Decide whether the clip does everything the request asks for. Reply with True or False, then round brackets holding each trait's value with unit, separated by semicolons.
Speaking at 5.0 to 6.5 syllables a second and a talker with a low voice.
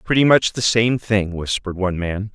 True (5.3 syllables/s; 105 Hz)